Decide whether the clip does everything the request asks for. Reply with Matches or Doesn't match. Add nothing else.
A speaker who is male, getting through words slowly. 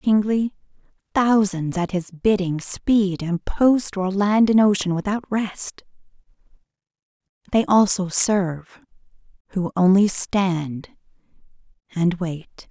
Doesn't match